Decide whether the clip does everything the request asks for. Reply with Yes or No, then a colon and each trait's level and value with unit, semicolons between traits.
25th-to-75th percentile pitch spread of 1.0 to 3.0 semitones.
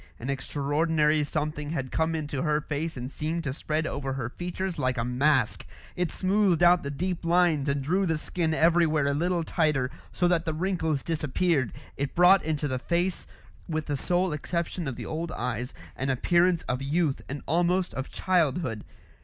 No: average, 3.7 semitones